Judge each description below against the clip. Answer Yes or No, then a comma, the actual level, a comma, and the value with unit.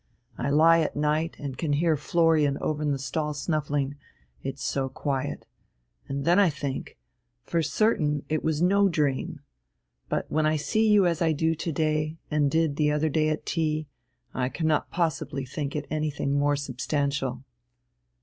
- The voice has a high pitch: No, medium, 150 Hz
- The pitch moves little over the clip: Yes, narrow, 2.2 semitones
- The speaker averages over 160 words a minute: Yes, average, 170 wpm